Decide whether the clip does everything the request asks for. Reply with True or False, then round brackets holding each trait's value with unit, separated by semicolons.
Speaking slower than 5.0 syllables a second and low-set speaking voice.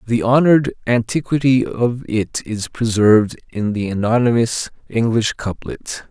True (4.3 syllables/s; 115 Hz)